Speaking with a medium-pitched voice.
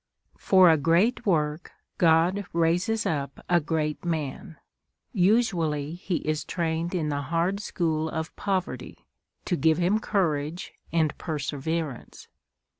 Yes: medium, 165 Hz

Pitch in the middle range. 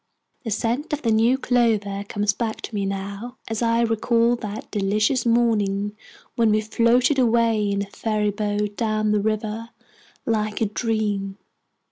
No: high, 220 Hz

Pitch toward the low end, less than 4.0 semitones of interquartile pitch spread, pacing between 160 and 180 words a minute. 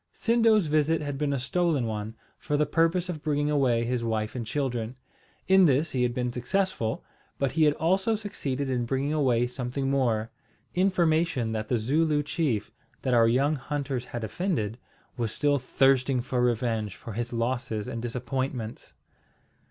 No: low, 130 Hz; average, 4.3 semitones; average, 165 wpm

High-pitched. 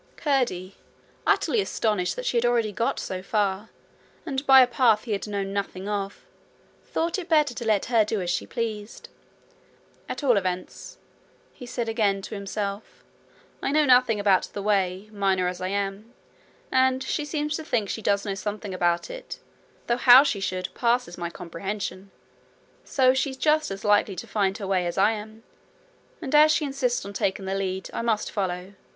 Yes: high, 210 Hz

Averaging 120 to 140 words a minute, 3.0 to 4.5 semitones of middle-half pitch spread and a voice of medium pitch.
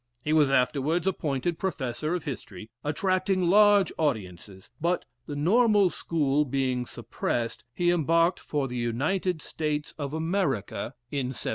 No: slow, 135 wpm; average, 5.2 semitones; medium, 150 Hz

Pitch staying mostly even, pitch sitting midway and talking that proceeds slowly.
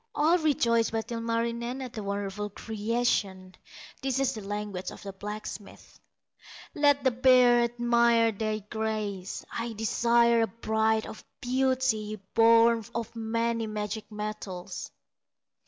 No: narrow, 2.1 semitones; high, 225 Hz; slow, 120 wpm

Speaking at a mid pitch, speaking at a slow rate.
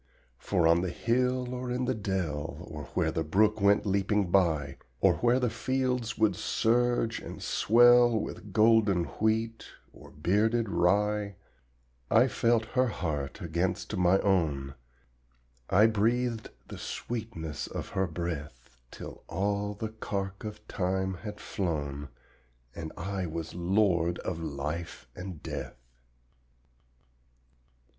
No: low, 100 Hz; slow, 125 wpm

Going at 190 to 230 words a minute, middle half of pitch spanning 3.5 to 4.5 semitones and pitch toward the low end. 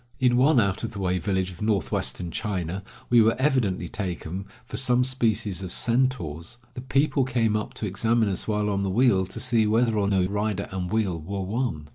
Yes: average, 200 wpm; average, 4.1 semitones; low, 105 Hz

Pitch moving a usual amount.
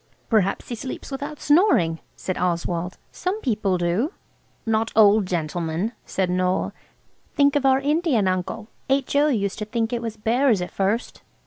No: wide, 6.7 semitones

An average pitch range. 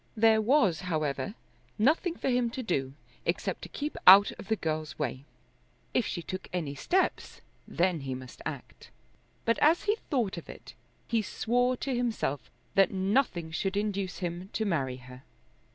No: wide, 6.8 semitones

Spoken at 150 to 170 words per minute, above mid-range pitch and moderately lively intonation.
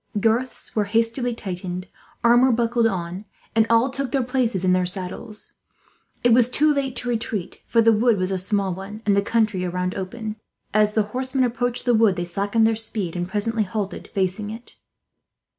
No: average, 180 wpm; high, 220 Hz; average, 3.8 semitones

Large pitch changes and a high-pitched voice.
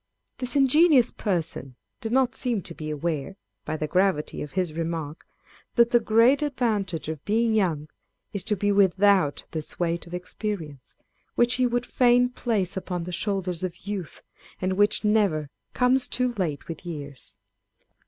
Yes: wide, 6.0 semitones; high, 195 Hz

